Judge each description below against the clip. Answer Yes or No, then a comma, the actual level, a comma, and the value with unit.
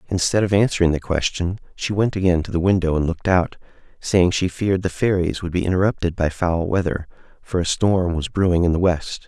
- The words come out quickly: Yes, fast, 215 wpm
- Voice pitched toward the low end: Yes, very low, 90 Hz